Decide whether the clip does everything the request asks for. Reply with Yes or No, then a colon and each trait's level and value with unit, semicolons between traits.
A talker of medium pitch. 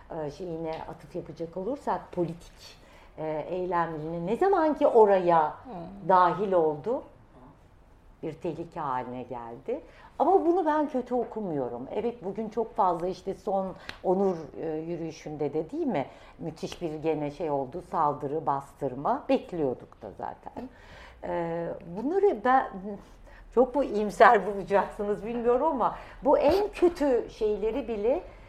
Yes: medium, 180 Hz